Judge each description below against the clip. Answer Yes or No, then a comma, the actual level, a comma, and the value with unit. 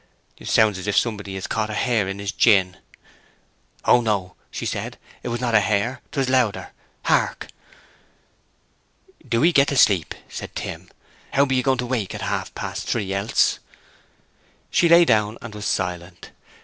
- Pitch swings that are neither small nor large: Yes, average, 4.1 semitones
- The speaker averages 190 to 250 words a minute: No, average, 170 wpm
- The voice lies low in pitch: Yes, low, 110 Hz